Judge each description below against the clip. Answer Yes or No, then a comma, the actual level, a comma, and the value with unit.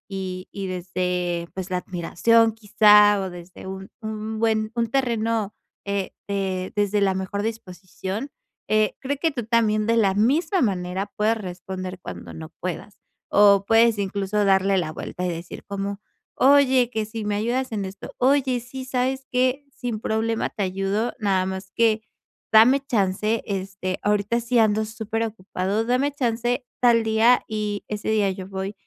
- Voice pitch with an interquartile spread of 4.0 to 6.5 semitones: No, average, 3.2 semitones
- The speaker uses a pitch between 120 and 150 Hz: No, high, 210 Hz